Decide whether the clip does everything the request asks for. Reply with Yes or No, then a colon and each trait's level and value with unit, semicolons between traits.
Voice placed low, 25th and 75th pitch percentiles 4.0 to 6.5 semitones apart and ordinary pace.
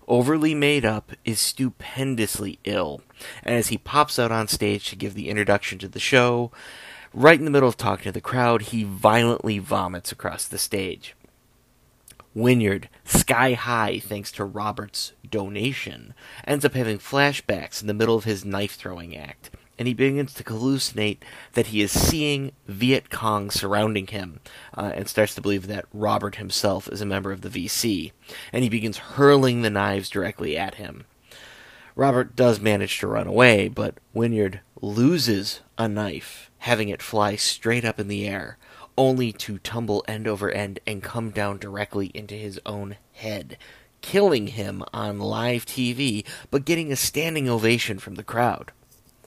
No: low, 110 Hz; average, 3.4 semitones; average, 165 wpm